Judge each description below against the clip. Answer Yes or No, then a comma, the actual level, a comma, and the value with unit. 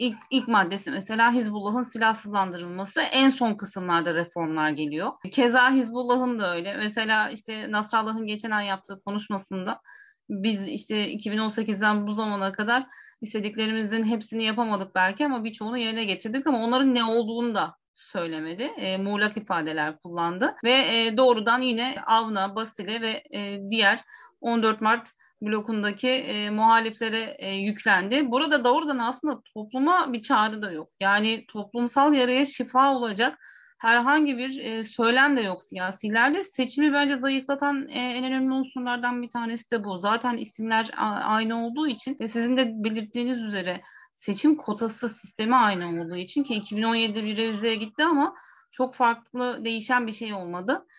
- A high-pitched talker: Yes, high, 225 Hz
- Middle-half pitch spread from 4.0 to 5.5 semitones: No, average, 3.4 semitones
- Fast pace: Yes, fast, 145 wpm